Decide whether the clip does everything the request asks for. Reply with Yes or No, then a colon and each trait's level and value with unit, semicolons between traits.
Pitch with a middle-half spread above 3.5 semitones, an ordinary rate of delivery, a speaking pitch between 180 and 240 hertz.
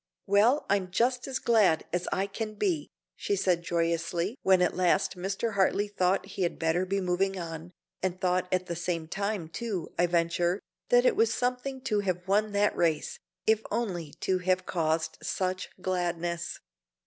No: average, 3.1 semitones; average, 170 wpm; medium, 185 Hz